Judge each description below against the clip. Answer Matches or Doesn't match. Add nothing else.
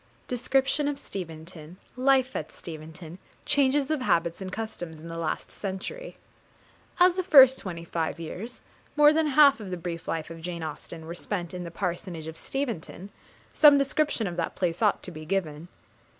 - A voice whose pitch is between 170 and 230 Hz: Matches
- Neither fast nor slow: Matches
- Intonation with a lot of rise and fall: Matches